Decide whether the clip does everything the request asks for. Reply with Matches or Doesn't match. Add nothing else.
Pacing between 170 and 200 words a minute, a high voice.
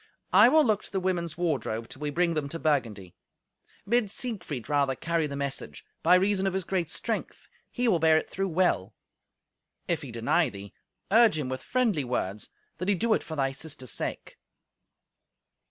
Doesn't match